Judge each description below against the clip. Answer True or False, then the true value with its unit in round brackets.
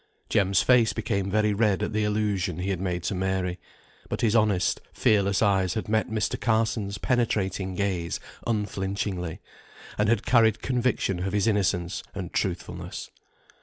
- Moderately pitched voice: False (100 Hz)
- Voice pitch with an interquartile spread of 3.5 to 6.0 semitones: False (2.5 semitones)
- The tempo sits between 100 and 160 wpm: True (145 wpm)